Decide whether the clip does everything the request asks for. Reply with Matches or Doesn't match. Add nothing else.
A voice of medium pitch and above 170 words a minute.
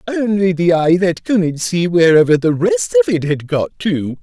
Matches